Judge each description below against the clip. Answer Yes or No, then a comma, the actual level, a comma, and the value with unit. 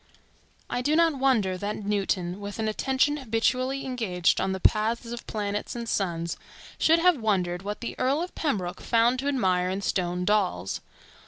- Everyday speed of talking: Yes, average, 170 wpm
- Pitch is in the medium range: No, high, 215 Hz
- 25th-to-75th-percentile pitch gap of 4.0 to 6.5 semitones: Yes, average, 5.3 semitones